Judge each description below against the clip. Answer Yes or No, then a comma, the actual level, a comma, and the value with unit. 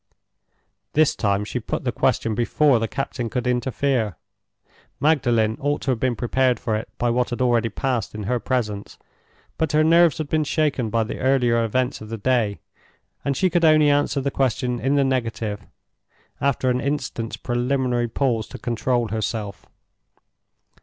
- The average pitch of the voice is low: Yes, low, 125 Hz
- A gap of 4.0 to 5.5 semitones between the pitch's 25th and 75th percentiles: No, average, 3.4 semitones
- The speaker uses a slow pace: No, average, 165 wpm